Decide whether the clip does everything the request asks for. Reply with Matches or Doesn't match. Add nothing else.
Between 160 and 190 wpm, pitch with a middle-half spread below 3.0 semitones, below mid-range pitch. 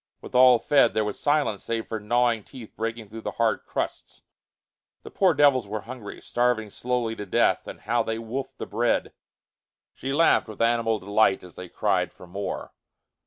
Matches